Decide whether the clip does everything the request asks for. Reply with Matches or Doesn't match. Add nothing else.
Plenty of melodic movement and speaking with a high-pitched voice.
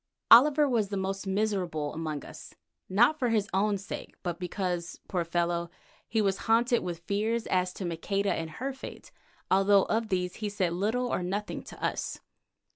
Doesn't match